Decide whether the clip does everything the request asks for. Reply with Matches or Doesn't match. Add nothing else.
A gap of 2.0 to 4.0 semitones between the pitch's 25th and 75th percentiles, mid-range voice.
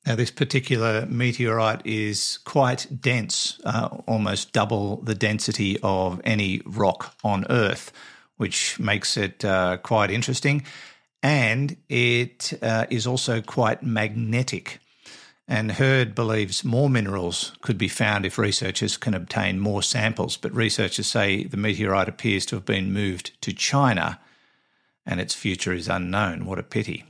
Doesn't match